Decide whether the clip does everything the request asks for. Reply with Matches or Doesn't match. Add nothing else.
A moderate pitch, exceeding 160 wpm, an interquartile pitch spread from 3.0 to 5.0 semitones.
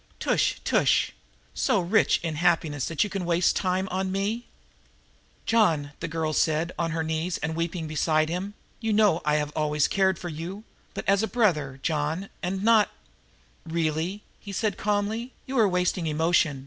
Matches